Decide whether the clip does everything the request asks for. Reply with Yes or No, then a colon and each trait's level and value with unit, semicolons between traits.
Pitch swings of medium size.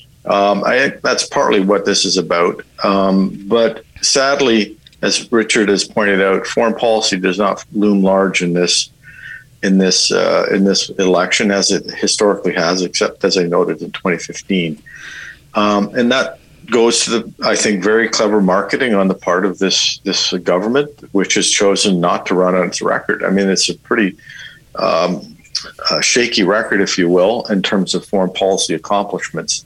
No: narrow, 2.1 semitones